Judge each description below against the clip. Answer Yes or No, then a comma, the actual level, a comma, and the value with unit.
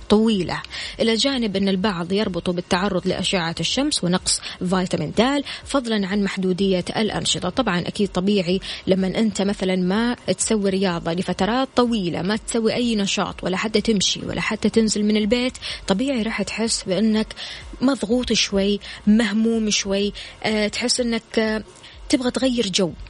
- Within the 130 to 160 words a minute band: Yes, fast, 135 wpm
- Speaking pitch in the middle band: No, high, 205 Hz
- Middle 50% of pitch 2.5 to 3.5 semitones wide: Yes, average, 3.2 semitones